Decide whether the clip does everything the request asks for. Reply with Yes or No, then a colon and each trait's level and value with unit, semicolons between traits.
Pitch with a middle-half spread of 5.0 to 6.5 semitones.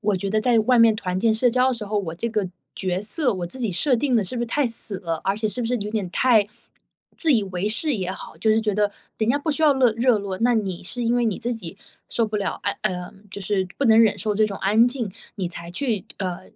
No: average, 3.5 semitones